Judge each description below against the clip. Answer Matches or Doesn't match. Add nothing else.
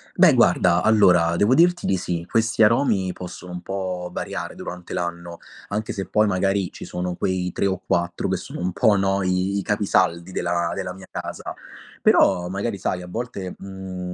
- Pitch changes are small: Matches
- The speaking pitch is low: Matches